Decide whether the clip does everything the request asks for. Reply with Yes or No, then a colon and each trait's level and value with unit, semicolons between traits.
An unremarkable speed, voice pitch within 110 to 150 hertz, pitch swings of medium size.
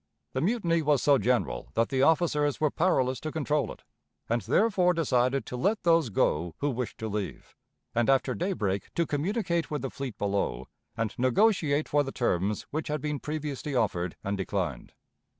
No: average, 175 wpm; medium, 140 Hz; wide, 5.9 semitones